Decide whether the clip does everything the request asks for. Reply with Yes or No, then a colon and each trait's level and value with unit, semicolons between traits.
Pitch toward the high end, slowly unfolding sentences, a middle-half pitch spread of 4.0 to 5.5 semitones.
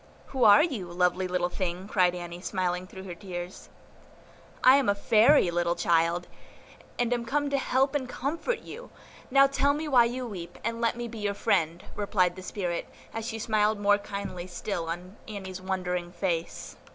No: high, 200 Hz; average, 180 wpm; average, 4.9 semitones